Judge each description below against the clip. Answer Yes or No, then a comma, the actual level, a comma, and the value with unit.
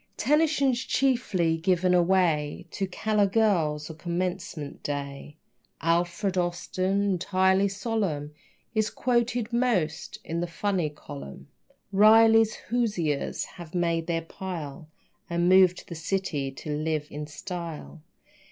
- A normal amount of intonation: Yes, average, 4.2 semitones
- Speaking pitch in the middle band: Yes, medium, 180 Hz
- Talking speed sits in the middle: No, slow, 115 wpm